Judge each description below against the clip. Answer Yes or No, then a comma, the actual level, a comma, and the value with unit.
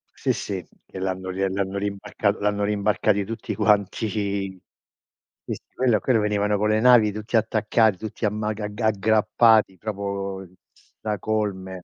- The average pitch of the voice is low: Yes, low, 105 Hz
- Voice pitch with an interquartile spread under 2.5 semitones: Yes, narrow, 1.8 semitones